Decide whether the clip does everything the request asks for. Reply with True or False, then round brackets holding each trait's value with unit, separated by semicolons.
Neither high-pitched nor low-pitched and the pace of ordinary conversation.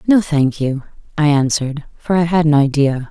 True (150 Hz; 195 wpm)